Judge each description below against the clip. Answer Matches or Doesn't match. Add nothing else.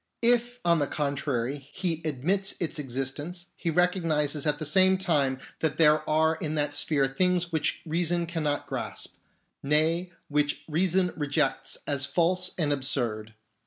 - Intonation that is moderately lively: Matches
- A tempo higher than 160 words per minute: Doesn't match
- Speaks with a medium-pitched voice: Matches